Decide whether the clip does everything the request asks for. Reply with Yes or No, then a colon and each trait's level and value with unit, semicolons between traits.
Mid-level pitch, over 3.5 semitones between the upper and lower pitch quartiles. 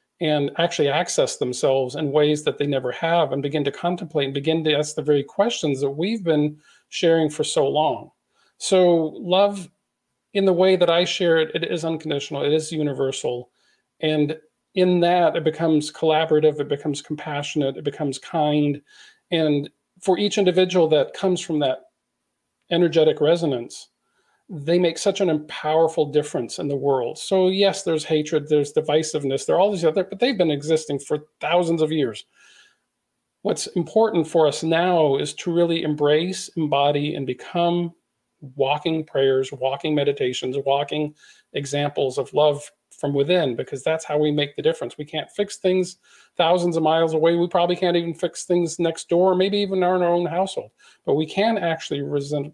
No: medium, 160 Hz; average, 3.0 semitones